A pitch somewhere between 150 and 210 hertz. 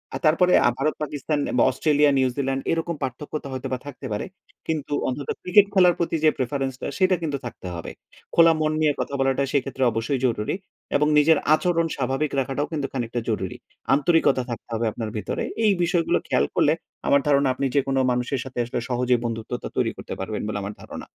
No: medium, 140 Hz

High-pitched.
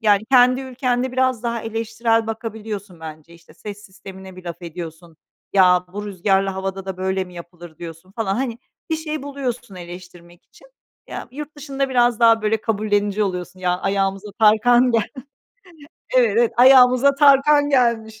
Yes: high, 215 Hz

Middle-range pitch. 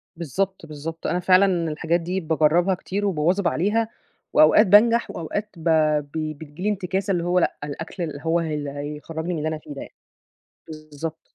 Yes: medium, 165 Hz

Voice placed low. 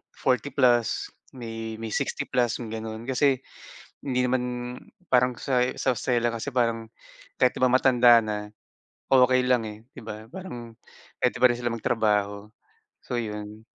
Yes: low, 120 Hz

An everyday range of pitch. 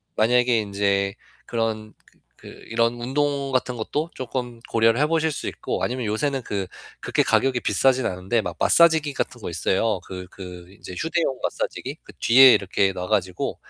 Yes: average, 5.0 semitones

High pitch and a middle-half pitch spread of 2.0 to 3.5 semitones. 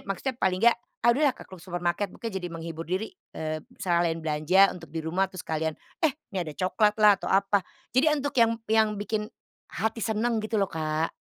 No: high, 195 Hz; average, 4.8 semitones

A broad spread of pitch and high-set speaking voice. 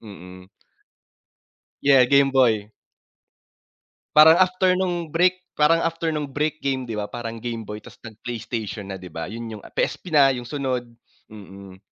No: wide, 6.1 semitones; low, 125 Hz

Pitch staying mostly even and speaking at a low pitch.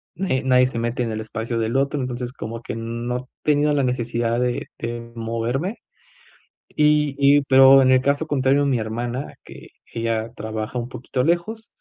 No: average, 3.0 semitones; low, 125 Hz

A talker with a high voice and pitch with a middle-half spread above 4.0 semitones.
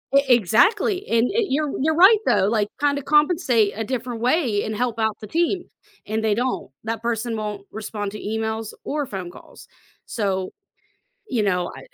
Yes: high, 230 Hz; average, 5.2 semitones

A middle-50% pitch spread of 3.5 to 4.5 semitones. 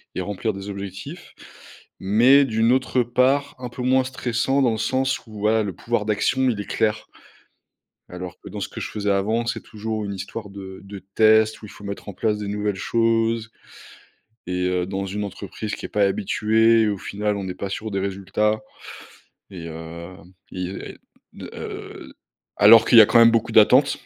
No: average, 2.8 semitones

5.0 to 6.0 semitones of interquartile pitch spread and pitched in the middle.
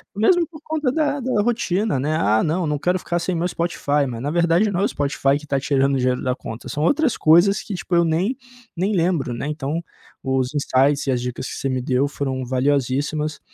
Yes: wide, 5.4 semitones; medium, 150 Hz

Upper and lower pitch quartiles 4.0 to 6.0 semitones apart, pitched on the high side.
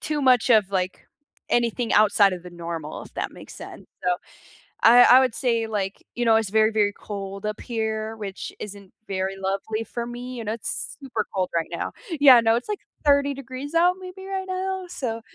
Yes: average, 4.4 semitones; high, 225 Hz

